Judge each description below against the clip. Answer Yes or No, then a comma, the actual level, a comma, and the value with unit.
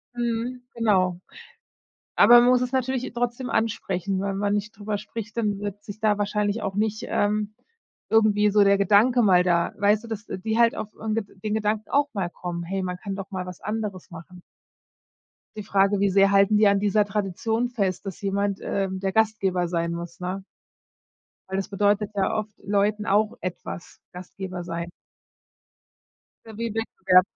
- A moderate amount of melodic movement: No, narrow, 2.3 semitones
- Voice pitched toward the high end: Yes, high, 205 Hz